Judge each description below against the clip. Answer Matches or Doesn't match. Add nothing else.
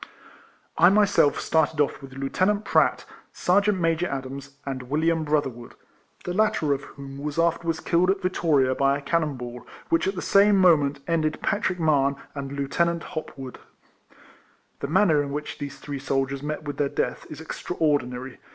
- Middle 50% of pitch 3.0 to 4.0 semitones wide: Matches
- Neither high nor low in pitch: Matches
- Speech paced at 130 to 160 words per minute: Doesn't match